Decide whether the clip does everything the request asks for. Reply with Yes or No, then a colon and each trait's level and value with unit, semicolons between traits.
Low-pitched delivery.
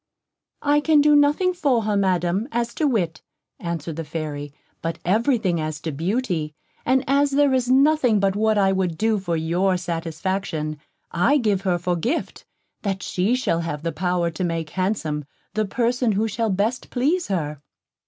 No: high, 195 Hz